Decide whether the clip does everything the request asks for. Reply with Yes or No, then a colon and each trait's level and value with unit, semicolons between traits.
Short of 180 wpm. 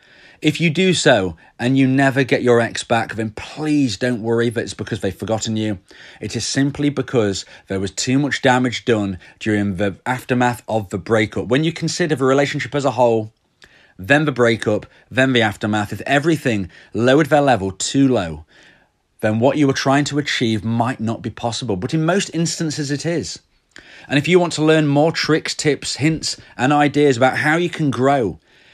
No: average, 190 wpm